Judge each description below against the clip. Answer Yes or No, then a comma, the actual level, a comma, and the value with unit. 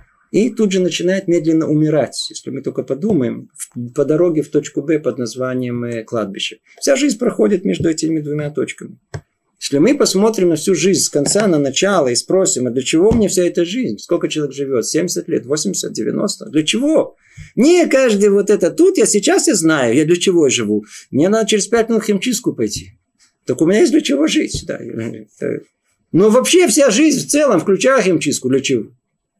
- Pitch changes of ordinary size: No, wide, 7.5 semitones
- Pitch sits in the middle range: Yes, medium, 180 Hz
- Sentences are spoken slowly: No, fast, 185 wpm